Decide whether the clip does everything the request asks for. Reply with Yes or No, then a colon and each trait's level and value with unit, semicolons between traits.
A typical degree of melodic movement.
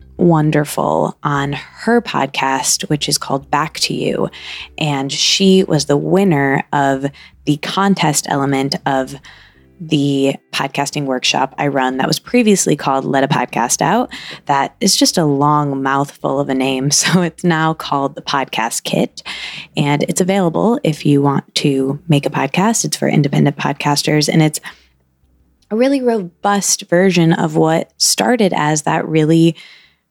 Yes: average, 4.1 semitones